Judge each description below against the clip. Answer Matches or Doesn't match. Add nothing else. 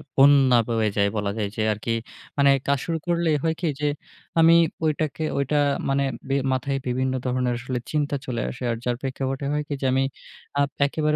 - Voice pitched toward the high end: Doesn't match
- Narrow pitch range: Doesn't match